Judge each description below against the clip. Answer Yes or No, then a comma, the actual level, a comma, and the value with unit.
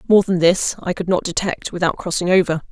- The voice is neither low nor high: Yes, medium, 180 Hz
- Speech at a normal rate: No, fast, 220 wpm